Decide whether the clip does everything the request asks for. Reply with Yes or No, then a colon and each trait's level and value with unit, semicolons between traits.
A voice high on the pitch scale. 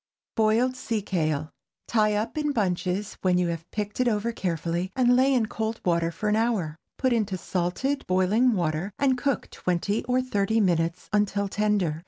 Yes: high, 210 Hz